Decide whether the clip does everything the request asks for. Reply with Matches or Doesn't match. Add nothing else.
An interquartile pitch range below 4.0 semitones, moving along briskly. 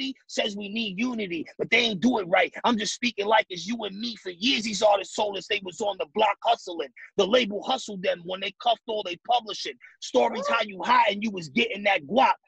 Matches